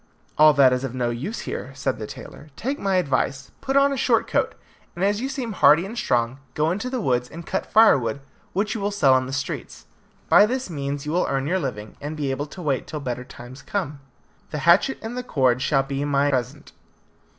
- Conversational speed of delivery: No, fast, 225 wpm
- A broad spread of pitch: Yes, wide, 7.1 semitones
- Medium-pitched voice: Yes, medium, 145 Hz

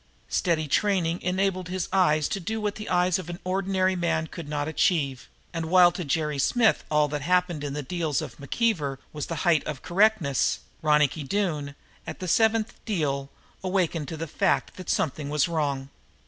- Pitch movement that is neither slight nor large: Yes, average, 3.9 semitones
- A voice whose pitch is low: No, medium, 170 Hz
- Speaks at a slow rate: No, average, 180 wpm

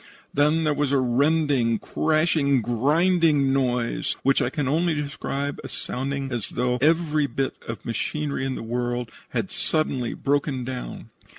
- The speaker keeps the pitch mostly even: No, average, 3.4 semitones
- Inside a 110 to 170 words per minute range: Yes, average, 150 wpm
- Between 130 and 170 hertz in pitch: Yes, medium, 140 Hz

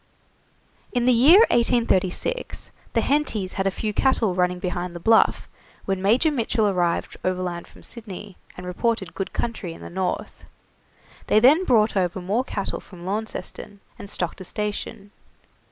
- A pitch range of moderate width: Yes, average, 4.3 semitones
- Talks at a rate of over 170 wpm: No, average, 155 wpm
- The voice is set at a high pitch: Yes, high, 200 Hz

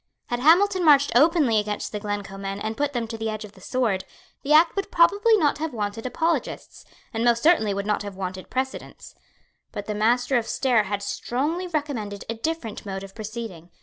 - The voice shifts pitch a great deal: Yes, wide, 6.4 semitones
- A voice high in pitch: Yes, high, 230 Hz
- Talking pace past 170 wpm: Yes, average, 200 wpm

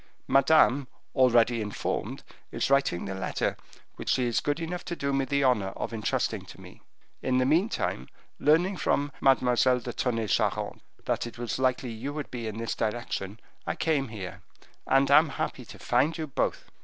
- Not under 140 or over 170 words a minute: No, average, 180 wpm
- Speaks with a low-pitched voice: Yes, low, 130 Hz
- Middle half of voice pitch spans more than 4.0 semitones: No, average, 3.5 semitones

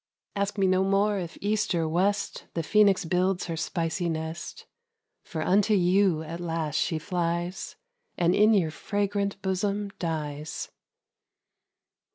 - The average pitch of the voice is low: No, medium, 180 Hz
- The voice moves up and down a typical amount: Yes, average, 3.3 semitones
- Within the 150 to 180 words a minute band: No, slow, 135 wpm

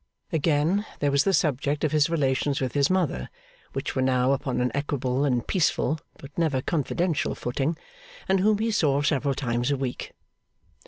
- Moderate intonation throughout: Yes, average, 3.4 semitones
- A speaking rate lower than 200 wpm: Yes, average, 170 wpm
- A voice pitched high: No, medium, 145 Hz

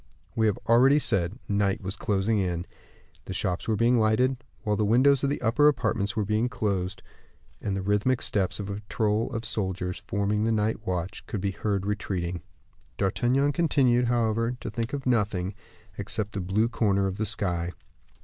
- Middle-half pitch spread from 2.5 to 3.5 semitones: Yes, average, 3.2 semitones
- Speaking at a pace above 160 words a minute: Yes, average, 180 wpm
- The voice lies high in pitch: No, low, 105 Hz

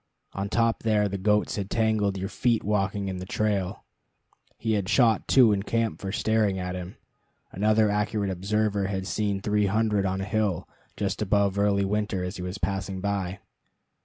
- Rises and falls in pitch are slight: Yes, narrow, 1.8 semitones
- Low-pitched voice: Yes, low, 100 Hz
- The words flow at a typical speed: Yes, average, 180 wpm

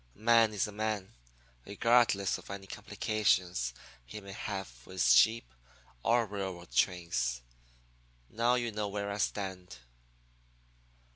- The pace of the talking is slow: Yes, slow, 125 wpm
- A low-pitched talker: Yes, low, 100 Hz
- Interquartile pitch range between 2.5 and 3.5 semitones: Yes, average, 3.1 semitones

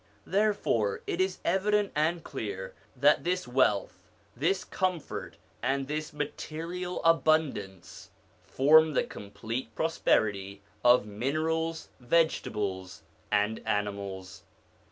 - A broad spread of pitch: Yes, wide, 8.1 semitones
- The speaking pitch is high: No, medium, 140 Hz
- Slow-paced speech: Yes, slow, 95 wpm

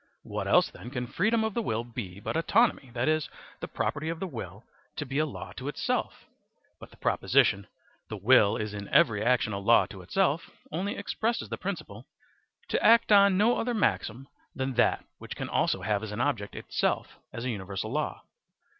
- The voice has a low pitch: Yes, low, 130 Hz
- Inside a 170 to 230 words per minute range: Yes, average, 195 wpm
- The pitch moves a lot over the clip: Yes, wide, 9.0 semitones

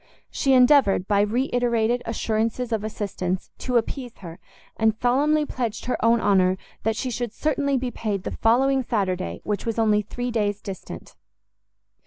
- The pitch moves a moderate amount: Yes, average, 3.2 semitones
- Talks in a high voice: Yes, high, 225 Hz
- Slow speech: No, average, 160 wpm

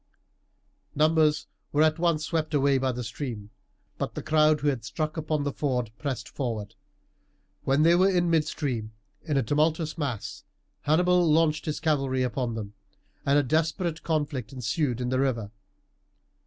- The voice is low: No, medium, 145 Hz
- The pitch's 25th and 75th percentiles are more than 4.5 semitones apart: No, average, 3.7 semitones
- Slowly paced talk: No, average, 155 wpm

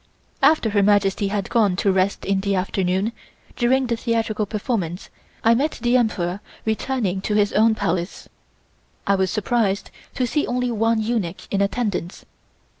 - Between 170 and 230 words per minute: No, average, 155 wpm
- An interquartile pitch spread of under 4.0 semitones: Yes, average, 3.2 semitones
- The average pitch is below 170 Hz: No, high, 210 Hz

